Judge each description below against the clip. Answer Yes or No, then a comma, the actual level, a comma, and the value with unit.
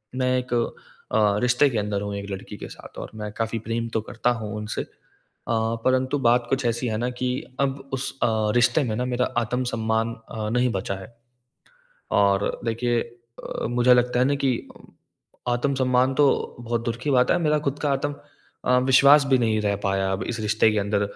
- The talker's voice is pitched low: Yes, low, 120 Hz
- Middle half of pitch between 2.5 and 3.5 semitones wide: Yes, average, 2.8 semitones